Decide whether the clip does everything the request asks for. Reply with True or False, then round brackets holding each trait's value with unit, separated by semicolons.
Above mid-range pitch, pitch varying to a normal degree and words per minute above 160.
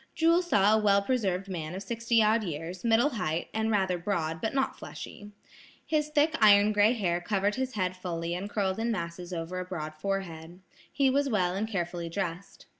True (195 Hz; 4.1 semitones; 190 wpm)